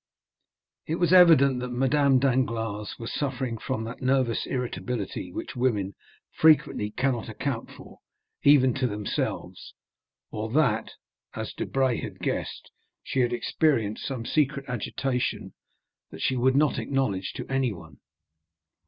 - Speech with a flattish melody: No, average, 3.3 semitones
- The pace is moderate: No, slow, 125 wpm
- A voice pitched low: Yes, low, 125 Hz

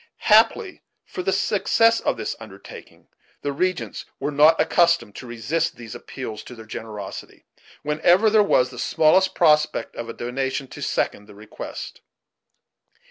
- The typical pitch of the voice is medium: Yes, medium, 150 Hz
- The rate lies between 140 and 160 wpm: Yes, average, 145 wpm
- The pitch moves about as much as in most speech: No, wide, 7.4 semitones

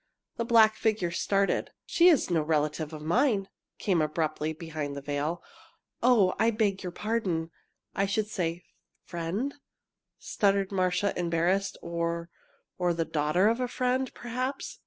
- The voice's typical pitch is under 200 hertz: Yes, medium, 185 Hz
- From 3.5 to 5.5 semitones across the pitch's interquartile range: Yes, average, 4.9 semitones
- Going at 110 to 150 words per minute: Yes, average, 145 wpm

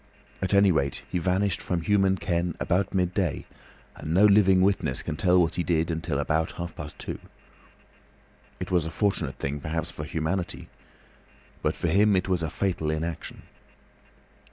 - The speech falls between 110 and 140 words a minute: No, average, 165 wpm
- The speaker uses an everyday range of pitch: Yes, average, 3.0 semitones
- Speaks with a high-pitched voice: No, very low, 85 Hz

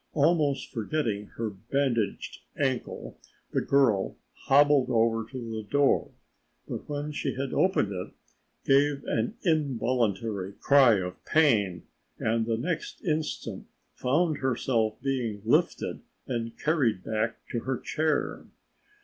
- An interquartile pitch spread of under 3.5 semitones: No, average, 4.4 semitones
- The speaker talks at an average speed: No, slow, 120 wpm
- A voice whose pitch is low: Yes, low, 125 Hz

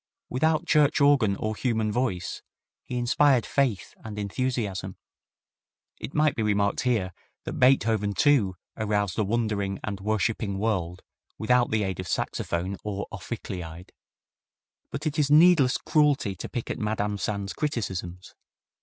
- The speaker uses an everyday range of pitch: Yes, average, 4.7 semitones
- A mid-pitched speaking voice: No, low, 110 Hz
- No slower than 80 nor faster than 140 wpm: Yes, slow, 135 wpm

